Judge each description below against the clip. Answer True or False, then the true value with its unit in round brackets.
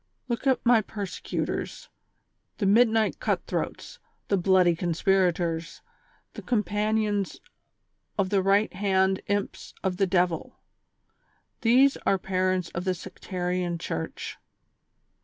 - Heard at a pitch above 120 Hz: True (190 Hz)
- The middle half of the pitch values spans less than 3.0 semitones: True (2.6 semitones)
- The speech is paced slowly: True (120 wpm)